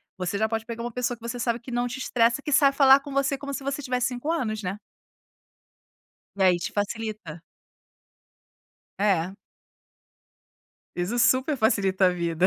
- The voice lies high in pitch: Yes, high, 235 Hz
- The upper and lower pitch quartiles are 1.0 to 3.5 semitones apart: No, average, 4.7 semitones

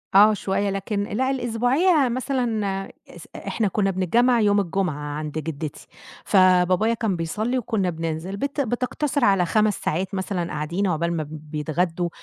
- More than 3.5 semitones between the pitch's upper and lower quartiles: Yes, average, 5.2 semitones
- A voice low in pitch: No, high, 195 Hz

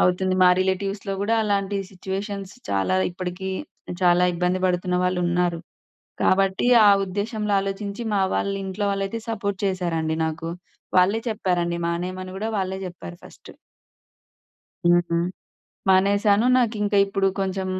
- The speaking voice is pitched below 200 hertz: Yes, high, 190 Hz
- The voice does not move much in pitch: Yes, narrow, 2.0 semitones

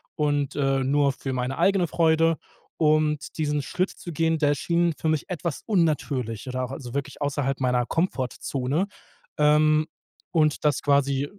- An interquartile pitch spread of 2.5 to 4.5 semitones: Yes, average, 2.9 semitones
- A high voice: No, medium, 150 Hz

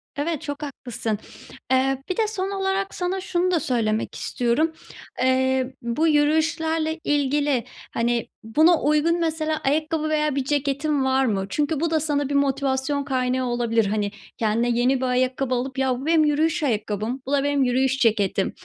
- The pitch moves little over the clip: No, average, 3.7 semitones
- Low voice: No, very high, 275 Hz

